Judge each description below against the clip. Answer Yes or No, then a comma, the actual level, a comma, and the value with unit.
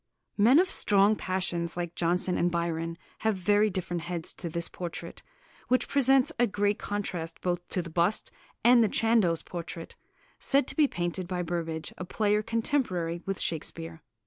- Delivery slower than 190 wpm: Yes, average, 165 wpm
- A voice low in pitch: No, medium, 180 Hz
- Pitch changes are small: No, average, 3.9 semitones